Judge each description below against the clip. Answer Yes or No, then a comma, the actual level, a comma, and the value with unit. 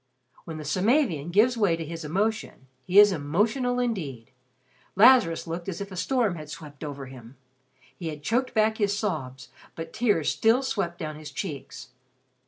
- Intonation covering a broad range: Yes, wide, 6.3 semitones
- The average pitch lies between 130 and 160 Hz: No, medium, 175 Hz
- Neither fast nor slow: Yes, average, 170 wpm